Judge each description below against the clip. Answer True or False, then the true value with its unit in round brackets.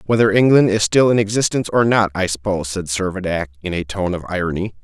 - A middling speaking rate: False (210 wpm)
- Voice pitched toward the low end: True (100 Hz)